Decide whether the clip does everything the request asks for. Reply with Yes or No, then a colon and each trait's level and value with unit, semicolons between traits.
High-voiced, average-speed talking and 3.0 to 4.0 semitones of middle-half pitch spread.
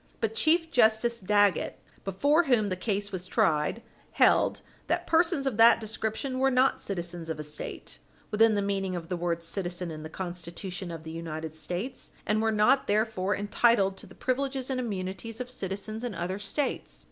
No: high, 205 Hz; average, 180 wpm; average, 5.0 semitones